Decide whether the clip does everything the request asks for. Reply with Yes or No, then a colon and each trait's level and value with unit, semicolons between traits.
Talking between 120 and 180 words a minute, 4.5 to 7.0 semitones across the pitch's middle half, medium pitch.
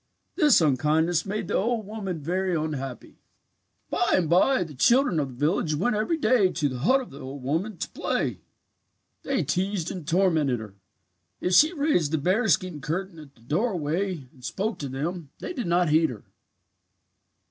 Yes: average, 175 wpm; average, 5.2 semitones; medium, 175 Hz